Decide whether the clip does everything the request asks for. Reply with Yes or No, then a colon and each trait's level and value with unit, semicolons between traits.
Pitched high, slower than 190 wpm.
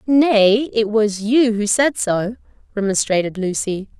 Yes: high, 220 Hz; slow, 135 wpm